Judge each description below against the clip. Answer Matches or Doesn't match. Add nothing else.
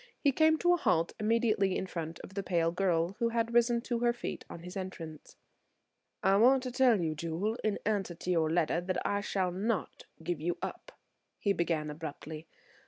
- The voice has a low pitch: Doesn't match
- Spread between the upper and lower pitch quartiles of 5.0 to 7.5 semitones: Matches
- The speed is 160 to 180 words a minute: Doesn't match